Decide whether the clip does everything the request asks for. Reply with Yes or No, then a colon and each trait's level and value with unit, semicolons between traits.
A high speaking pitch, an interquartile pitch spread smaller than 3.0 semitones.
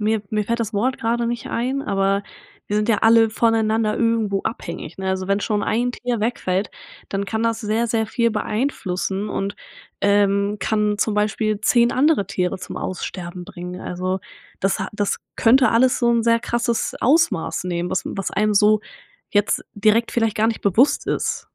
Yes: high, 215 Hz; narrow, 2.6 semitones